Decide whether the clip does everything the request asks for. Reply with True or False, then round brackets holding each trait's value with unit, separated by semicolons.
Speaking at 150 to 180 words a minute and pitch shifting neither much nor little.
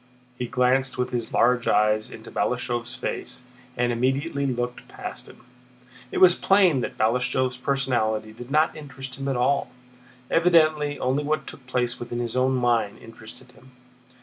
False (155 wpm; 2.3 semitones)